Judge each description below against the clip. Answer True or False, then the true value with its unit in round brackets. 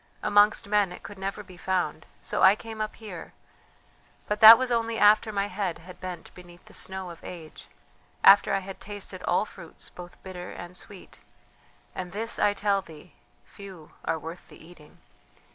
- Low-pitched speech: False (190 Hz)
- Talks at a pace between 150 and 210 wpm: True (180 wpm)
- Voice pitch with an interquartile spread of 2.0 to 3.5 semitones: True (2.7 semitones)